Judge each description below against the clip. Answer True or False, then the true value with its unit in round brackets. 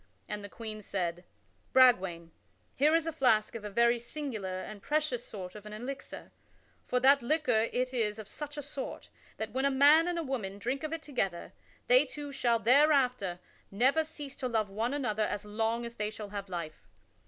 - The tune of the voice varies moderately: True (5.0 semitones)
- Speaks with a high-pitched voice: True (235 Hz)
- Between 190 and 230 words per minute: True (195 wpm)